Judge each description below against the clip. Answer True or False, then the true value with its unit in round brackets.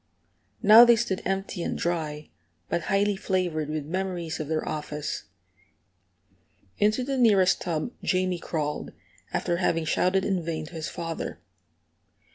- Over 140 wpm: False (135 wpm)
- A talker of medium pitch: True (175 Hz)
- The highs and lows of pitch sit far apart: False (3.4 semitones)